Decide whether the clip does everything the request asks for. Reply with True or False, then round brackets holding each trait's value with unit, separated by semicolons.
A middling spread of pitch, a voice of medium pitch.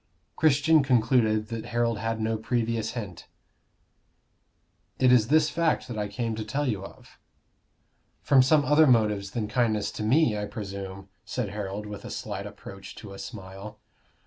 False (3.4 semitones; 110 Hz)